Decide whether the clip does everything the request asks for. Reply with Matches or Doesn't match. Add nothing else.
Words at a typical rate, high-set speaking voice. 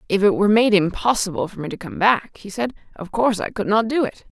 Doesn't match